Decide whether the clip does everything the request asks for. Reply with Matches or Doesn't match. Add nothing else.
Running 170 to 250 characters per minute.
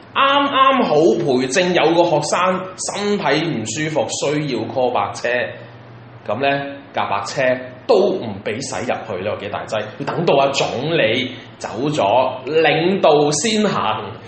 Matches